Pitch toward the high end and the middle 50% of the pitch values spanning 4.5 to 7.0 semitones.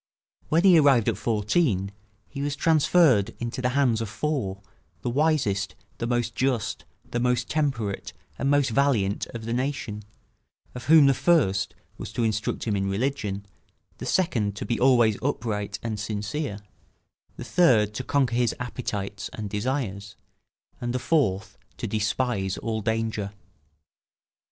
No: low, 120 Hz; average, 4.8 semitones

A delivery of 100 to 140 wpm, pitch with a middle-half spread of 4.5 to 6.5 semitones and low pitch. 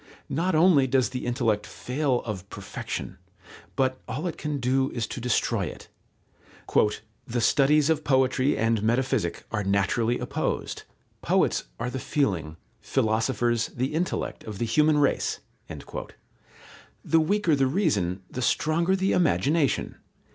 Yes: slow, 135 wpm; average, 4.9 semitones; low, 130 Hz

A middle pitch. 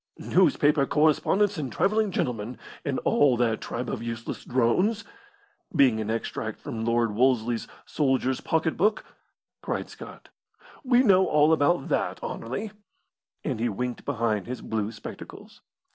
No: low, 130 Hz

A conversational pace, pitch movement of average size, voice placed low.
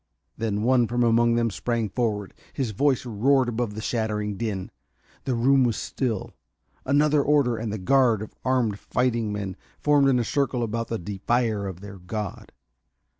Yes: average, 170 wpm; average, 3.3 semitones; low, 115 Hz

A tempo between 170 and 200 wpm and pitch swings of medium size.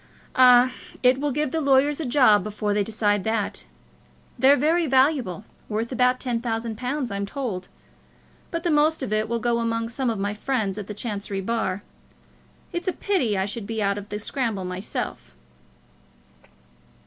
Yes: average, 175 wpm; average, 4.3 semitones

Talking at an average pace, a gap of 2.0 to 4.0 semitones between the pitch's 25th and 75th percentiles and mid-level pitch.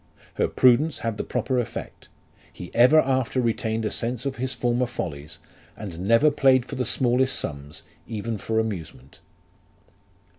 No: average, 150 wpm; average, 3.4 semitones; low, 120 Hz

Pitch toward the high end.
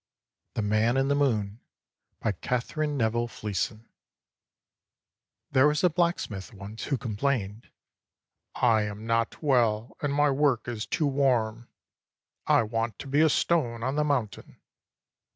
No: low, 120 Hz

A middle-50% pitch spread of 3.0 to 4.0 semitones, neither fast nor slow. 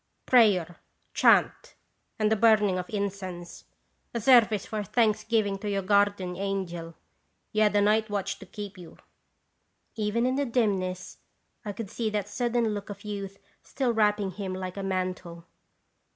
No: narrow, 2.4 semitones; average, 155 wpm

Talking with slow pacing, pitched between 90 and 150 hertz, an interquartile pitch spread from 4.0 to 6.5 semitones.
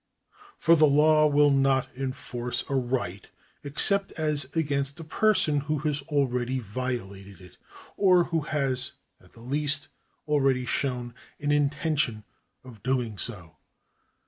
No: slow, 130 wpm; medium, 140 Hz; average, 3.3 semitones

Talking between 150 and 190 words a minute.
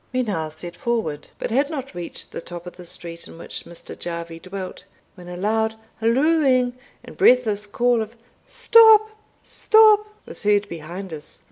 Yes: average, 165 wpm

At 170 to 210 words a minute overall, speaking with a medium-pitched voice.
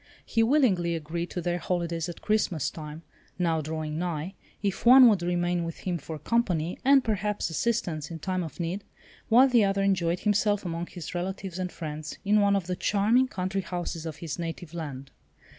Yes: average, 185 wpm; medium, 175 Hz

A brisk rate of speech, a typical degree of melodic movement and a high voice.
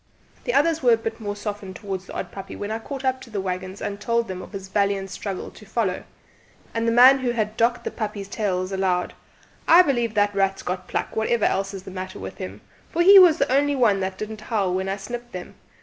Yes: fast, 240 wpm; average, 3.7 semitones; high, 205 Hz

